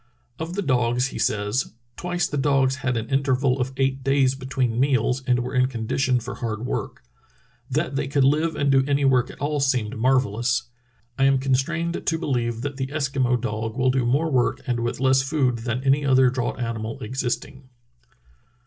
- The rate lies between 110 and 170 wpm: No, average, 185 wpm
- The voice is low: Yes, low, 130 Hz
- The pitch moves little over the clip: Yes, narrow, 2.1 semitones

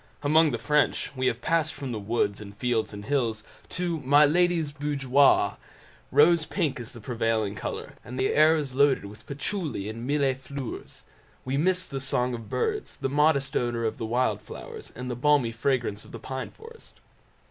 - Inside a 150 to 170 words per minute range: No, average, 180 wpm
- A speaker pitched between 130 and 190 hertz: Yes, low, 135 Hz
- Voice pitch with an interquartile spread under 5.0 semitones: Yes, average, 4.2 semitones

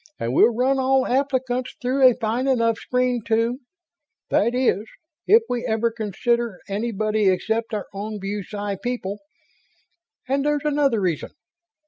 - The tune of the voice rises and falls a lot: No, average, 3.3 semitones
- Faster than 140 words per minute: No, slow, 135 wpm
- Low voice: No, high, 235 Hz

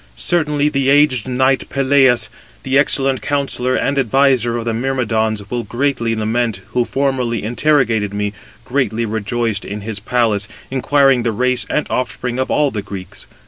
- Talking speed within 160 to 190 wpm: No, average, 150 wpm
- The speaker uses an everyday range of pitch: Yes, average, 3.4 semitones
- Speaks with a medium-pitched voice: No, low, 125 Hz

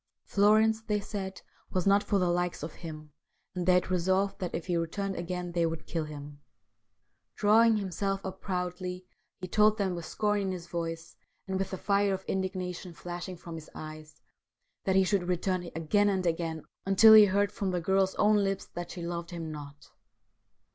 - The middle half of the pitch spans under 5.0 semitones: Yes, narrow, 2.6 semitones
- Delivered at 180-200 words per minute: Yes, average, 190 wpm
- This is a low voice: No, medium, 185 Hz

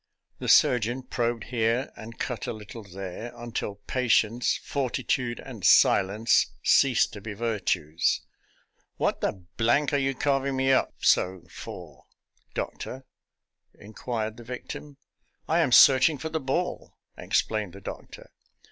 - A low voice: Yes, low, 120 Hz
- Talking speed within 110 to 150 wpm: Yes, average, 140 wpm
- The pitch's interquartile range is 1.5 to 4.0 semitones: Yes, average, 3.6 semitones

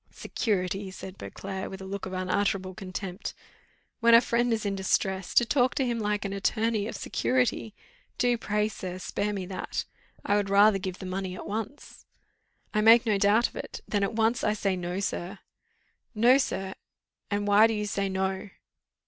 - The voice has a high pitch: Yes, high, 200 Hz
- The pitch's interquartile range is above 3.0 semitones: No, narrow, 2.6 semitones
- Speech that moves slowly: No, average, 185 wpm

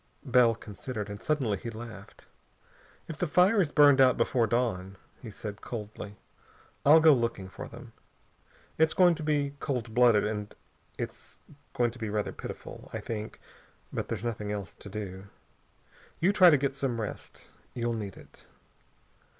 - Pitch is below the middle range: Yes, low, 115 Hz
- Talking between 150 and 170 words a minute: Yes, average, 160 wpm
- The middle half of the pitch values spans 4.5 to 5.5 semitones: Yes, average, 5.2 semitones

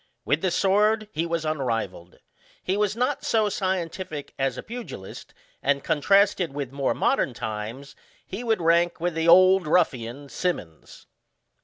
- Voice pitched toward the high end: No, medium, 165 Hz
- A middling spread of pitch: No, wide, 5.8 semitones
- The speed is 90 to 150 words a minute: Yes, average, 145 wpm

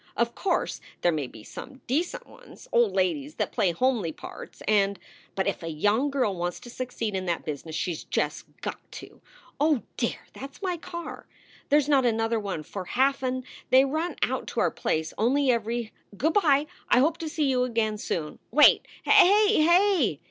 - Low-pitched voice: No, high, 240 Hz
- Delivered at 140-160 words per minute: No, average, 190 wpm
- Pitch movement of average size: No, wide, 7.2 semitones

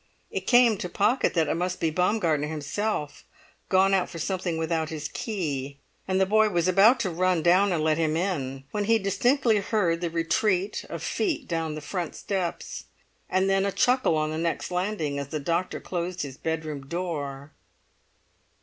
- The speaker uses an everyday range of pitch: Yes, average, 3.8 semitones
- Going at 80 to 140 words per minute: No, average, 180 wpm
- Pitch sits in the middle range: Yes, medium, 175 Hz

